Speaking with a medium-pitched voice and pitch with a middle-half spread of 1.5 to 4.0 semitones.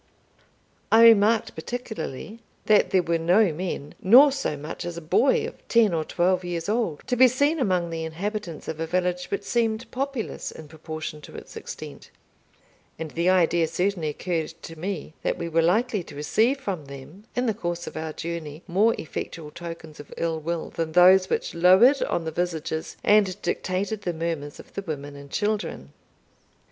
No: medium, 175 Hz; average, 4.7 semitones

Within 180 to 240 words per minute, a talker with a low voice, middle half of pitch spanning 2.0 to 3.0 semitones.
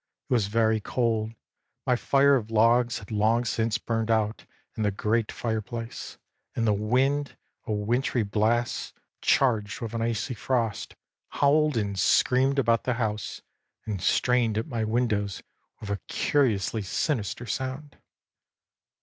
No: average, 140 wpm; low, 115 Hz; narrow, 2.6 semitones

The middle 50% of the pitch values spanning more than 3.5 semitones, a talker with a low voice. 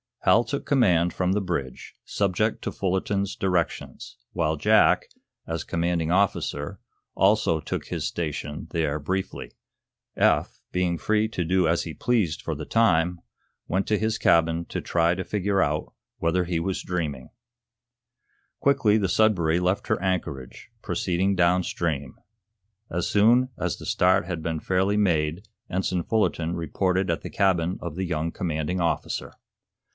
No: average, 2.9 semitones; very low, 90 Hz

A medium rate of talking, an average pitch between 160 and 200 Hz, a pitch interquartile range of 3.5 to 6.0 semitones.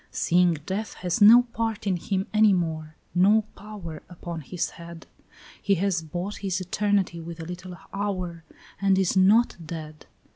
No: average, 155 wpm; medium, 185 Hz; average, 3.1 semitones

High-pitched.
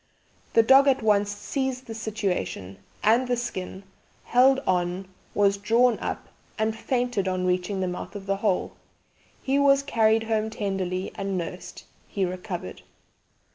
Yes: high, 205 Hz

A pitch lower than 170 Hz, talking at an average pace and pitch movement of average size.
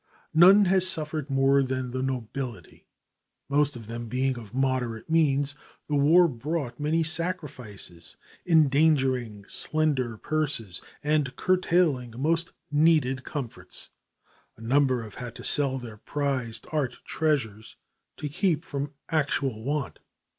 No: medium, 140 Hz; slow, 125 wpm; average, 4.0 semitones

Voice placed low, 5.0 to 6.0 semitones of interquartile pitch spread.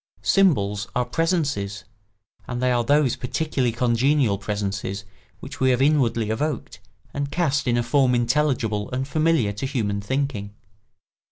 Yes: low, 125 Hz; average, 5.3 semitones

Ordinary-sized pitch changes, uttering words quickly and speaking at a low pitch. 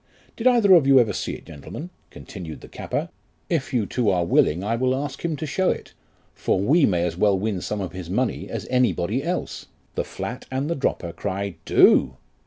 No: wide, 7.0 semitones; fast, 210 wpm; low, 115 Hz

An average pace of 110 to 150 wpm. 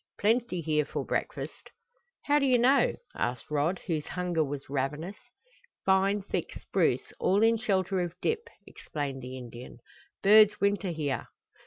Yes: average, 145 wpm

